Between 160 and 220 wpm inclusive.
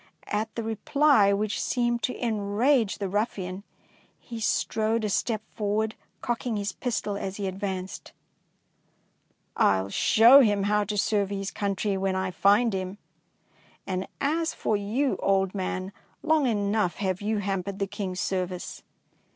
No: average, 145 wpm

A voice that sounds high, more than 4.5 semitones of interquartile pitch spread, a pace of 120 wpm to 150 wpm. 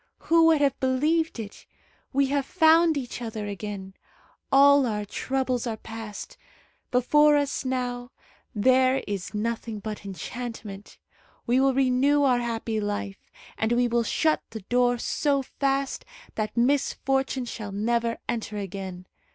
No: high, 245 Hz; average, 4.0 semitones; slow, 135 wpm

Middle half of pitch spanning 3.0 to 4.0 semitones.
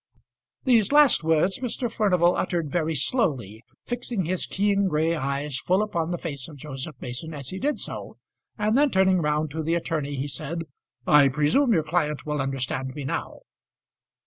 No: average, 4.9 semitones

